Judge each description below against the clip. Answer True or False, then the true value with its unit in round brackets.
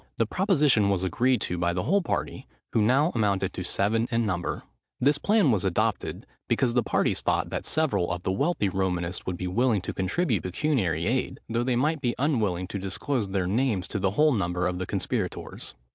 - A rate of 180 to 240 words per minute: True (200 wpm)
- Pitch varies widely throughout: True (6.0 semitones)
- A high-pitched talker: False (105 Hz)